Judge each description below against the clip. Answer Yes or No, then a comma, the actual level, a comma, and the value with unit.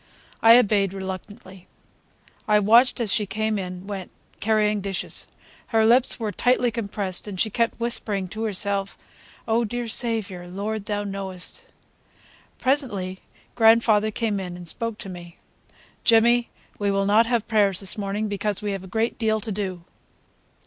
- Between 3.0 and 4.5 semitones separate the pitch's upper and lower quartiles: No, narrow, 2.5 semitones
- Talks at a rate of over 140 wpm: Yes, average, 155 wpm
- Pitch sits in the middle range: No, high, 210 Hz